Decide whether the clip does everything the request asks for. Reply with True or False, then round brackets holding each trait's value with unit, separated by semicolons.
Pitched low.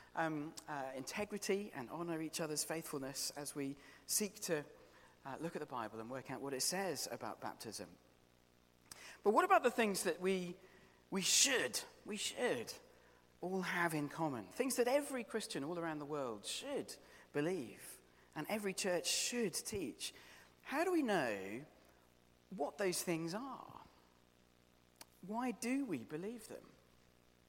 False (165 Hz)